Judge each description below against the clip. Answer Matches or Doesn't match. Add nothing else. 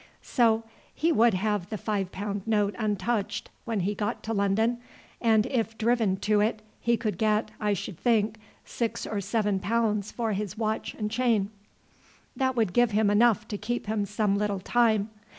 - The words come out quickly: Doesn't match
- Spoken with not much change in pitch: Matches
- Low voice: Doesn't match